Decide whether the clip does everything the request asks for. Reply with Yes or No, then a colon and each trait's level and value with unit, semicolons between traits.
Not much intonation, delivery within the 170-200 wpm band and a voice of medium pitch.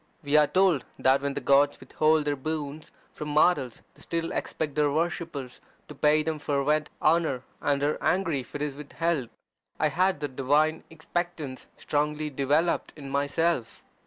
No: narrow, 2.3 semitones; average, 160 wpm; medium, 150 Hz